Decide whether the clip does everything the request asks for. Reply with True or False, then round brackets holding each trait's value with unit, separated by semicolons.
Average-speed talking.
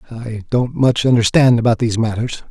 True (165 wpm)